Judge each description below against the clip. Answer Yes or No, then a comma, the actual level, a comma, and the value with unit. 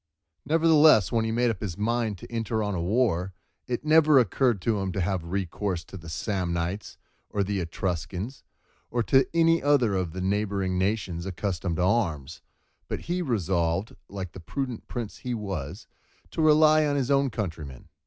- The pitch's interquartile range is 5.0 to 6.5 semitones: Yes, average, 5.3 semitones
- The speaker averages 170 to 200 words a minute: Yes, average, 175 wpm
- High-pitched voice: No, low, 100 Hz